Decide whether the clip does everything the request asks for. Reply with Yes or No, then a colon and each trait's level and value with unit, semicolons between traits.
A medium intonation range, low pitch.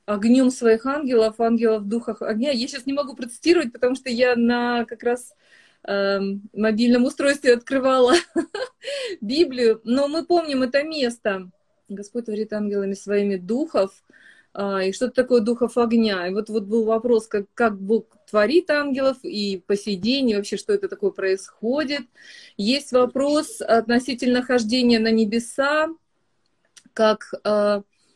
No: average, 4.1 semitones; high, 240 Hz